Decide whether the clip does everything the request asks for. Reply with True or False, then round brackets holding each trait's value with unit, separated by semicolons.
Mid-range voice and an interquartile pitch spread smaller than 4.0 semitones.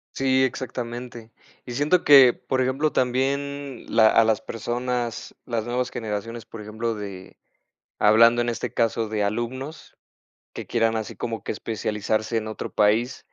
False (115 Hz; 2.7 semitones)